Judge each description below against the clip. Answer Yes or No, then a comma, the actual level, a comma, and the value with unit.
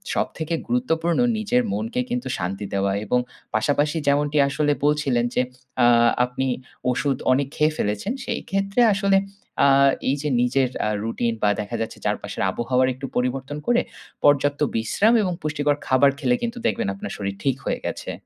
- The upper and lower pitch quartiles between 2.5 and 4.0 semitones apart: No, average, 4.8 semitones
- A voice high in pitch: No, medium, 140 Hz